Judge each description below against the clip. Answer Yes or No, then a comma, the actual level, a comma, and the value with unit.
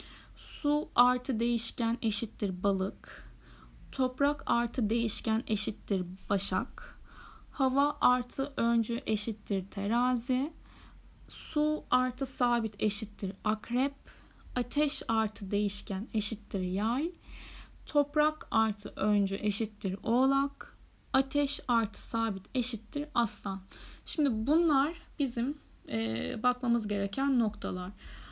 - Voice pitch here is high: Yes, high, 235 Hz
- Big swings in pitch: No, average, 4.2 semitones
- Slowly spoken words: Yes, slow, 85 wpm